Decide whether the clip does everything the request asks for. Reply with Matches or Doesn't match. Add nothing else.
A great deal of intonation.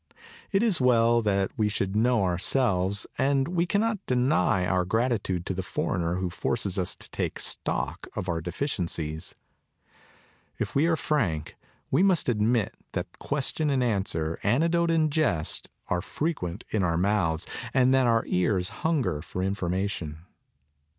Matches